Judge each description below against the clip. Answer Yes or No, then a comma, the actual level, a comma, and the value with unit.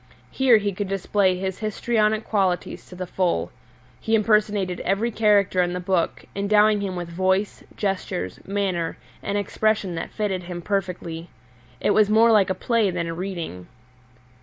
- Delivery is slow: No, average, 160 wpm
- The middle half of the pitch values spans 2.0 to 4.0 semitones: Yes, average, 2.7 semitones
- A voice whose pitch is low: No, high, 195 Hz